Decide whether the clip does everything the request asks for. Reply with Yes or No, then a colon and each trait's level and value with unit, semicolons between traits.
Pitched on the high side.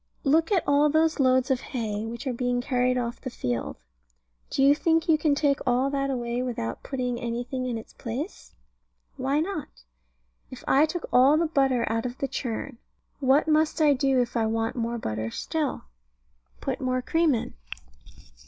Yes: very high, 260 Hz